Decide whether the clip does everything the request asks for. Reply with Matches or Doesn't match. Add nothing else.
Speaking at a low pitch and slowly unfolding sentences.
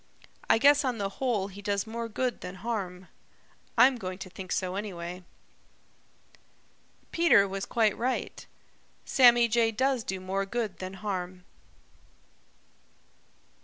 Doesn't match